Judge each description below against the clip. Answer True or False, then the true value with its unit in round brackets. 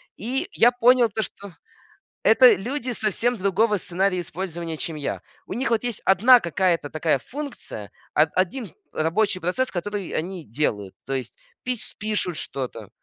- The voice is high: True (195 Hz)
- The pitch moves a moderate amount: False (6.1 semitones)